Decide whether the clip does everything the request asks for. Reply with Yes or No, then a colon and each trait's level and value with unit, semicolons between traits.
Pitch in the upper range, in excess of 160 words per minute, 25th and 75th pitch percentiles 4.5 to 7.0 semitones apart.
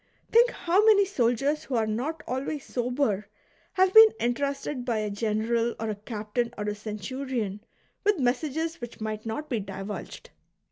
No: high, 245 Hz; average, 155 wpm; wide, 5.4 semitones